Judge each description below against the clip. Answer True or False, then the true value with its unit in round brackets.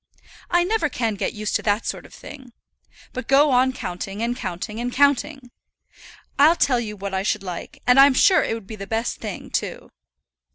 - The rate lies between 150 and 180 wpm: False (200 wpm)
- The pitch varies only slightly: False (4.5 semitones)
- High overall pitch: True (240 Hz)